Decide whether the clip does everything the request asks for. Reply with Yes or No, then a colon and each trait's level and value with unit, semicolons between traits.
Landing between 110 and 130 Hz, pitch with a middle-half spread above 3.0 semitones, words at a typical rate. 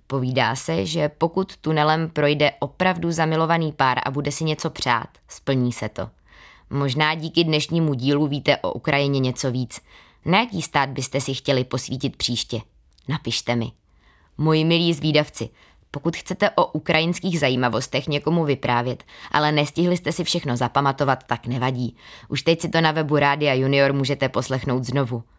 No: medium, 140 Hz; average, 3.9 semitones; average, 155 wpm